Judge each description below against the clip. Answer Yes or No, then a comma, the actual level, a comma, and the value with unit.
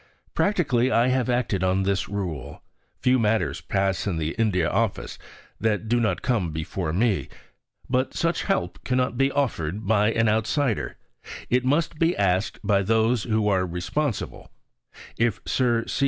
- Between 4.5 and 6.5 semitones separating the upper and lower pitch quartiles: Yes, average, 4.8 semitones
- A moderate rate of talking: Yes, average, 155 wpm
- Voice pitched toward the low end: Yes, low, 110 Hz